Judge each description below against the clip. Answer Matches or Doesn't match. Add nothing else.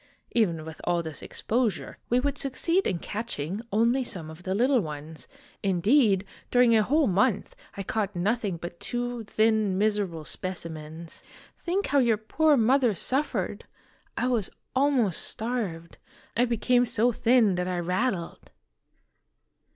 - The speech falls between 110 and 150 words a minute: Matches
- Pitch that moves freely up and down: Matches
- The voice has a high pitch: Matches